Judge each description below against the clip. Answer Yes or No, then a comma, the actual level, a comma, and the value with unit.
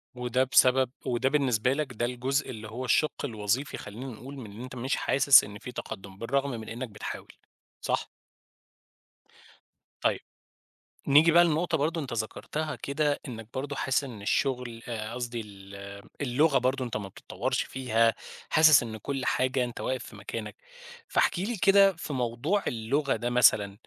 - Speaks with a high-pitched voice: No, low, 125 Hz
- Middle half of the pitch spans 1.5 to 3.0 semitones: No, average, 3.6 semitones